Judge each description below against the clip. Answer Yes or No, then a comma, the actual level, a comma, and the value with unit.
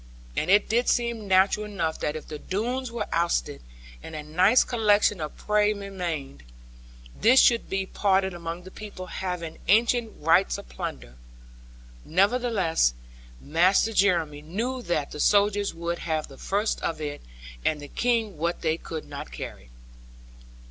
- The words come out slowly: No, average, 150 wpm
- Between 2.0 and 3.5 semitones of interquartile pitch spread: No, average, 4.8 semitones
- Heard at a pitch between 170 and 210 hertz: Yes, medium, 185 Hz